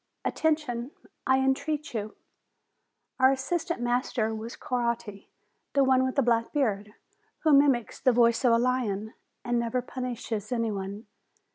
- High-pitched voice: Yes, high, 240 Hz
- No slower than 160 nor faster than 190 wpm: No, average, 140 wpm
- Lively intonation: No, narrow, 2.6 semitones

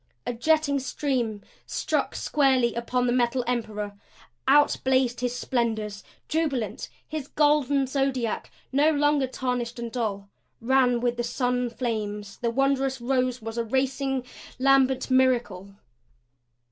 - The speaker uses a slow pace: Yes, slow, 120 wpm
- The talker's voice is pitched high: Yes, very high, 250 Hz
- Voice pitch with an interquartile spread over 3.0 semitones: No, narrow, 2.4 semitones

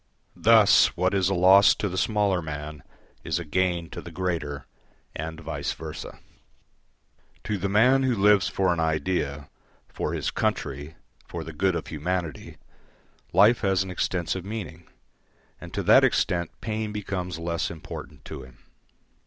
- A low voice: Yes, very low, 90 Hz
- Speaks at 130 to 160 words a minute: Yes, average, 155 wpm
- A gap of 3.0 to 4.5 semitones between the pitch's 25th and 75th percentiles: Yes, average, 3.5 semitones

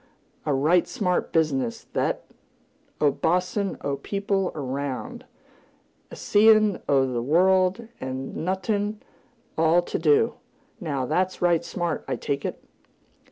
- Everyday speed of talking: No, slow, 125 wpm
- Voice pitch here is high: No, medium, 170 Hz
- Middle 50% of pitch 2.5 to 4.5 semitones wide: No, average, 5.3 semitones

